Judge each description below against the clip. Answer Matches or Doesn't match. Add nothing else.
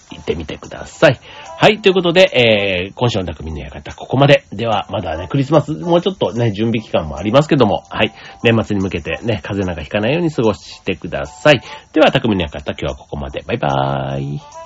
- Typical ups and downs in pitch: Doesn't match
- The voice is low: Matches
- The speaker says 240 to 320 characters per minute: Doesn't match